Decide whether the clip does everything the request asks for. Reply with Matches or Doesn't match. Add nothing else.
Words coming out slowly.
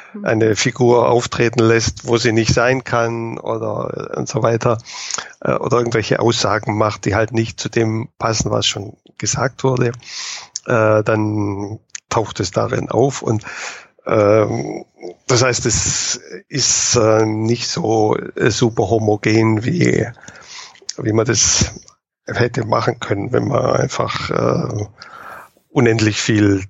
Matches